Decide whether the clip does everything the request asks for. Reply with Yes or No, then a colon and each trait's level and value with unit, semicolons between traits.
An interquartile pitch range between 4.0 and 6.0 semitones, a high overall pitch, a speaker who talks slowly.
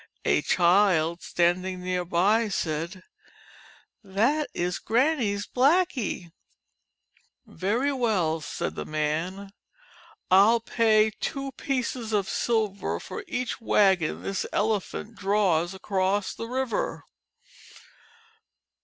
Yes: average, 4.3 semitones; high, 200 Hz; slow, 100 wpm